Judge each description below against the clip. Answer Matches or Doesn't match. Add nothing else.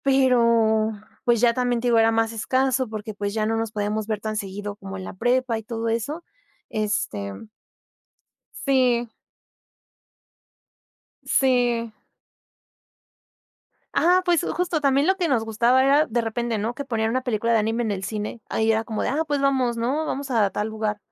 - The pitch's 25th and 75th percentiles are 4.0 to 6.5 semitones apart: Doesn't match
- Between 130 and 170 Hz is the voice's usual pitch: Doesn't match